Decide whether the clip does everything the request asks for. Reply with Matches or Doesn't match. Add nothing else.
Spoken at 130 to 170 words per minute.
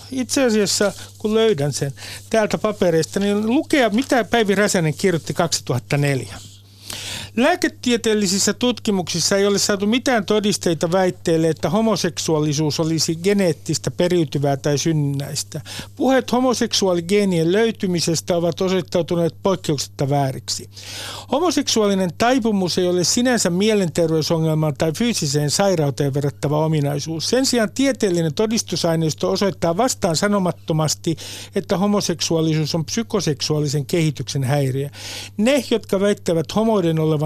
Doesn't match